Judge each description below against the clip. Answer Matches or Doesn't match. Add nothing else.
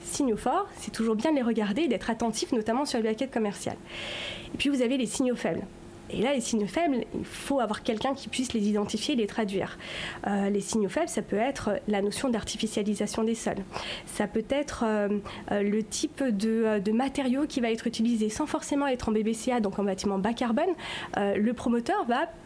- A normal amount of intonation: Matches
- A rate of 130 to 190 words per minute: Doesn't match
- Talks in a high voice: Matches